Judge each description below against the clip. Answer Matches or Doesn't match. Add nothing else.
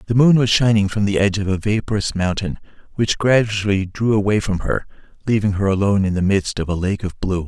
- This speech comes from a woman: Doesn't match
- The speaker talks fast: Matches